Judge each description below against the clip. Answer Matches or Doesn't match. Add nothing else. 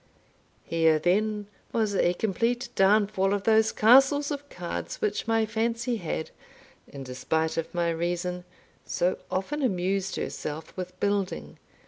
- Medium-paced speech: Doesn't match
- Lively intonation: Doesn't match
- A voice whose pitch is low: Doesn't match